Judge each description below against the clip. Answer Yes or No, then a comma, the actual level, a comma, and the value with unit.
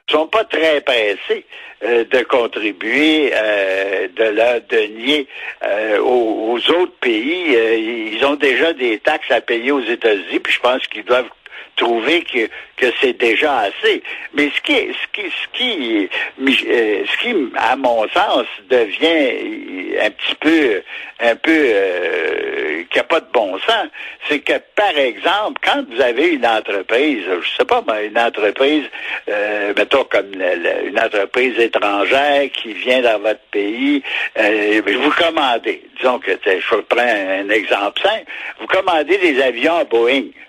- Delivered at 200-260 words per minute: No, average, 155 wpm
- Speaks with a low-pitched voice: No, very high, 360 Hz